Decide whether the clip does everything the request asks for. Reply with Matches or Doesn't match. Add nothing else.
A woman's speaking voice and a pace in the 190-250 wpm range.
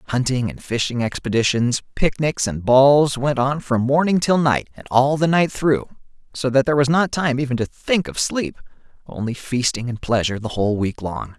Doesn't match